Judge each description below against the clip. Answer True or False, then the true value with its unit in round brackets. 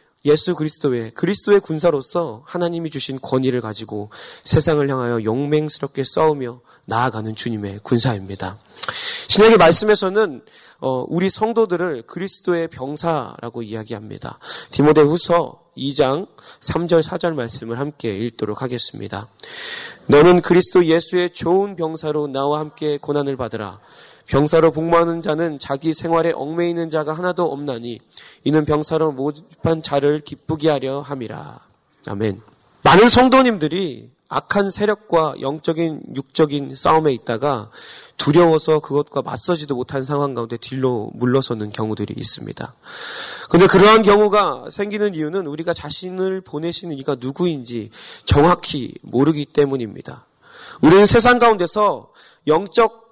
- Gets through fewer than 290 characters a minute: False (320 characters per minute)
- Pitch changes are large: False (4.9 semitones)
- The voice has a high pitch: False (150 Hz)